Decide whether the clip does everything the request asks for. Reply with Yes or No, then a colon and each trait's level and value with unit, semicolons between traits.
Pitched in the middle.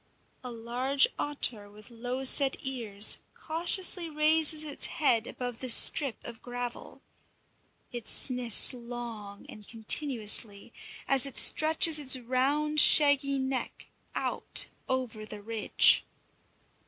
No: very high, 255 Hz